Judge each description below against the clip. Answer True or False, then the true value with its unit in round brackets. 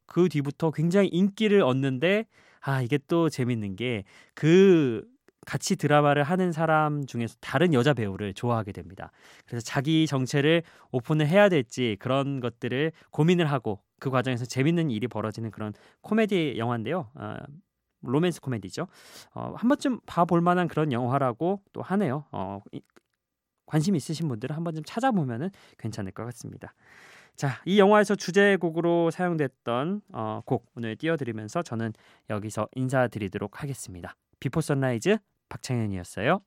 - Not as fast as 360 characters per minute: True (335 characters per minute)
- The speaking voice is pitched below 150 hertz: True (140 Hz)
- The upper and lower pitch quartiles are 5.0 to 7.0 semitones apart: True (6.4 semitones)